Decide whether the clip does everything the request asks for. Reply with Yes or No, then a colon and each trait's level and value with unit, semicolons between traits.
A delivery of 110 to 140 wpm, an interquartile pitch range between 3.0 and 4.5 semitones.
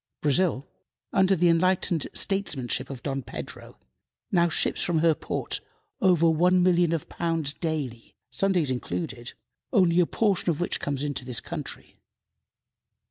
Yes: slow, 135 wpm; average, 4.1 semitones